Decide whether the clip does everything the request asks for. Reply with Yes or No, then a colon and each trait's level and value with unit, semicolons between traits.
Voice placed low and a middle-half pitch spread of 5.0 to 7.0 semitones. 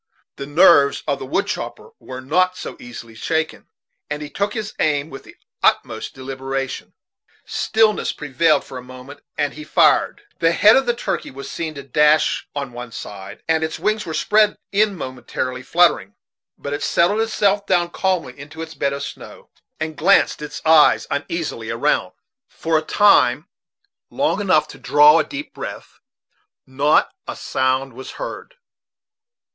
No: medium, 150 Hz; wide, 5.5 semitones